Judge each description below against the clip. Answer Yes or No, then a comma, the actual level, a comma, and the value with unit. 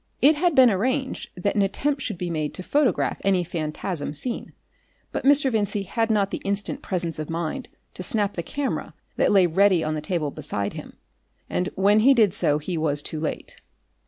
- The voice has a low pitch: No, high, 195 Hz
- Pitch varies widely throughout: Yes, wide, 5.8 semitones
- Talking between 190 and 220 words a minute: Yes, average, 195 wpm